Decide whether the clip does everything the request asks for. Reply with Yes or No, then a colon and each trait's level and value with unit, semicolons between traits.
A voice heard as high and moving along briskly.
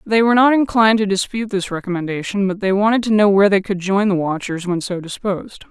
Yes: high, 200 Hz; fast, 230 wpm